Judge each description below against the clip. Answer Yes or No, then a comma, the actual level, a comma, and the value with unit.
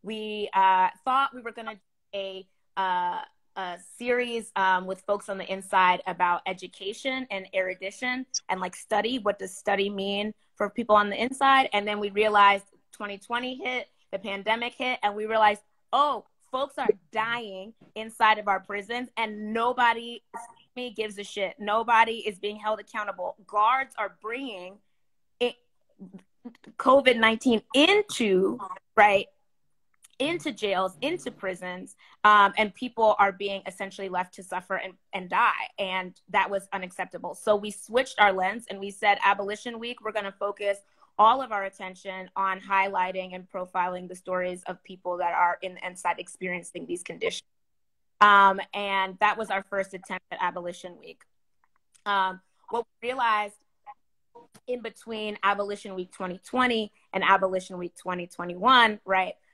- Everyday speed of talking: Yes, average, 150 wpm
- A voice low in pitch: No, high, 205 Hz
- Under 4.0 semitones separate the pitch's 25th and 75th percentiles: Yes, average, 3.4 semitones